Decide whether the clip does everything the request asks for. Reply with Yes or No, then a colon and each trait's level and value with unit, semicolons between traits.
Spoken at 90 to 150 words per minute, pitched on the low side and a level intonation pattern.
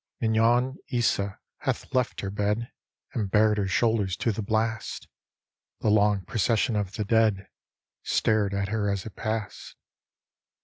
Yes: average, 140 wpm; low, 110 Hz; narrow, 2.0 semitones